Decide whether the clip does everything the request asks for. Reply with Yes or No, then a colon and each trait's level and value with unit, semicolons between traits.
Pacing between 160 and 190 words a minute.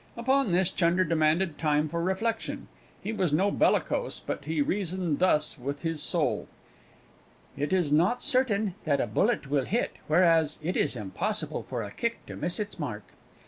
Yes: average, 170 wpm